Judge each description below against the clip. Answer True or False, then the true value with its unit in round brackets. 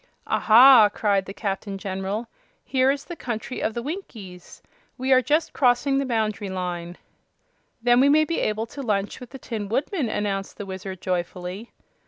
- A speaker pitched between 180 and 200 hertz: False (220 Hz)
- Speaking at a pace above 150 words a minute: True (170 wpm)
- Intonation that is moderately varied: True (5.0 semitones)